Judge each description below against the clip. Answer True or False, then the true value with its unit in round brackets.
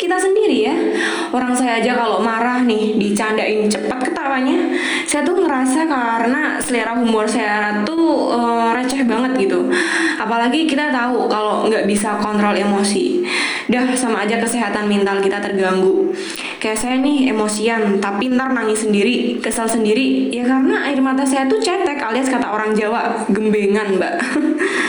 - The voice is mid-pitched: False (235 Hz)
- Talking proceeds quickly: True (145 wpm)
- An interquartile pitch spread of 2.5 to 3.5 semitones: False (4.3 semitones)